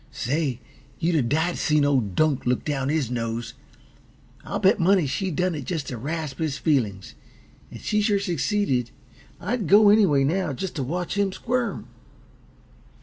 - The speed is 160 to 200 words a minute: Yes, average, 165 wpm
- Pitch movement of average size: No, wide, 6.1 semitones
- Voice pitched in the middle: Yes, medium, 155 Hz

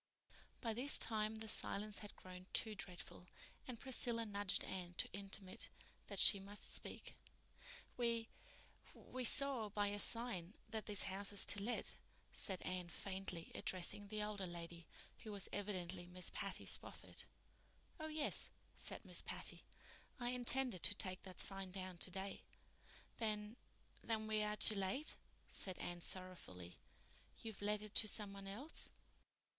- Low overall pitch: No, high, 205 Hz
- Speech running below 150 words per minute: Yes, average, 140 wpm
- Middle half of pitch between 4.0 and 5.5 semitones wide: No, average, 2.9 semitones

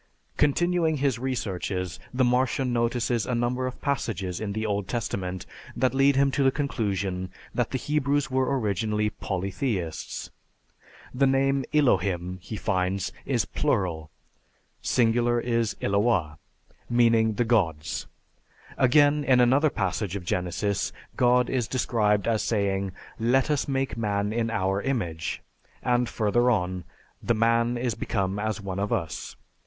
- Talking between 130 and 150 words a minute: Yes, average, 140 wpm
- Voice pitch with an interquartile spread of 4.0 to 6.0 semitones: Yes, average, 4.7 semitones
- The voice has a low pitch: Yes, low, 115 Hz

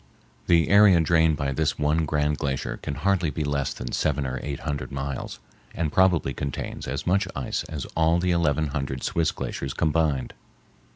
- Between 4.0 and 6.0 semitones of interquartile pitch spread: No, average, 3.0 semitones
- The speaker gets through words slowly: No, average, 175 wpm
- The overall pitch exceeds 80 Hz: No, very low, 75 Hz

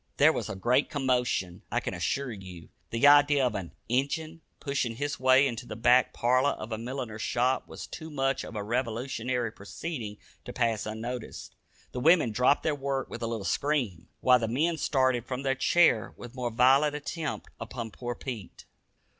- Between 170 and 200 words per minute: Yes, average, 180 wpm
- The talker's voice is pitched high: No, low, 125 Hz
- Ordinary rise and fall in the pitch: Yes, average, 3.4 semitones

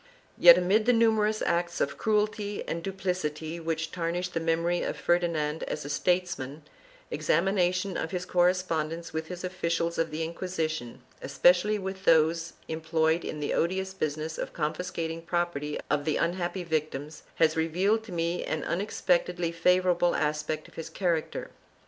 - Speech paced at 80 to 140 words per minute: No, average, 155 wpm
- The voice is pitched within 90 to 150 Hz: No, medium, 170 Hz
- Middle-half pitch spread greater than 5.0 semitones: No, narrow, 2.4 semitones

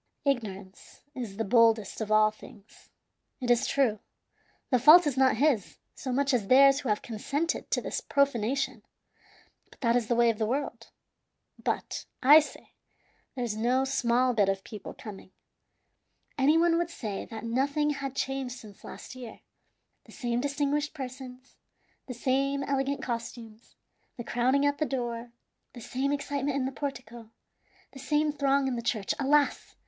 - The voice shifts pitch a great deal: No, average, 3.3 semitones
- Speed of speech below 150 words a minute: No, average, 160 wpm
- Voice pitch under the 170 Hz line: No, very high, 255 Hz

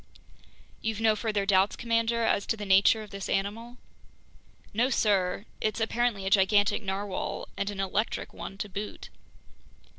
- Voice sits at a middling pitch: No, high, 205 Hz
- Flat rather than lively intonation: Yes, narrow, 2.3 semitones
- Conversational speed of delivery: Yes, average, 150 wpm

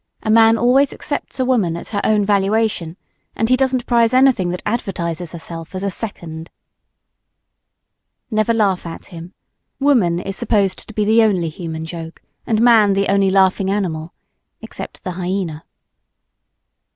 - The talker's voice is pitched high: Yes, high, 195 Hz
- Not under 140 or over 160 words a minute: Yes, average, 150 wpm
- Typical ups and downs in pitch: Yes, average, 4.5 semitones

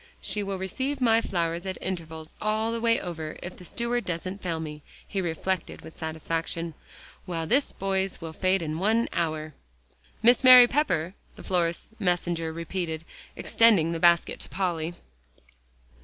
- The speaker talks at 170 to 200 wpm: No, average, 155 wpm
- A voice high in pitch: No, medium, 175 Hz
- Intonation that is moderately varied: Yes, average, 4.0 semitones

